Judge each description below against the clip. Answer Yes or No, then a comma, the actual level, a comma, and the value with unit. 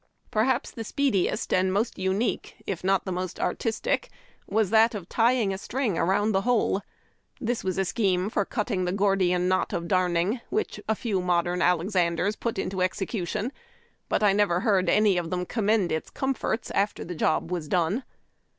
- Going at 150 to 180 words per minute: Yes, average, 175 wpm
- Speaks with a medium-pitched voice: No, high, 195 Hz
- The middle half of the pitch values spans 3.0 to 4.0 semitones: Yes, average, 3.4 semitones